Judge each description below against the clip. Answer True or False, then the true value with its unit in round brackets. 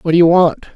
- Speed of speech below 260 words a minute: False (315 wpm)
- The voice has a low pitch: False (170 Hz)